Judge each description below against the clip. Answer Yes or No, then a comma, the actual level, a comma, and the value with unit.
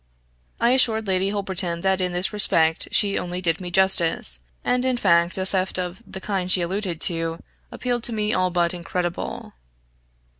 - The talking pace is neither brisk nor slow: Yes, average, 175 wpm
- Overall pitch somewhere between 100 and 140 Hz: No, medium, 185 Hz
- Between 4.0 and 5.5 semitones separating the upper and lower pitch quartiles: No, narrow, 2.6 semitones